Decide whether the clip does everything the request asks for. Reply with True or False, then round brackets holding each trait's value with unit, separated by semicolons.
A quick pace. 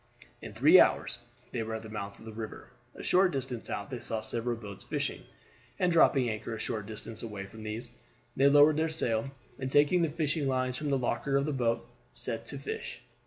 True (215 wpm)